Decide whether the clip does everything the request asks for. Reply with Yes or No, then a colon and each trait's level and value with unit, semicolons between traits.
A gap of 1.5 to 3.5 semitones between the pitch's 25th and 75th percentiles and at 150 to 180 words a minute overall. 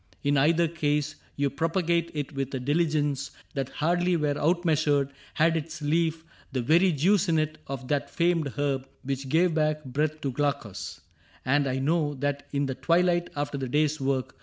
Yes: average, 2.9 semitones; average, 175 wpm